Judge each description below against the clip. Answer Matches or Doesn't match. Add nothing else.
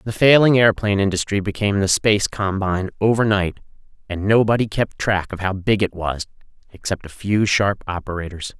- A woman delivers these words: Doesn't match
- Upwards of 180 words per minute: Doesn't match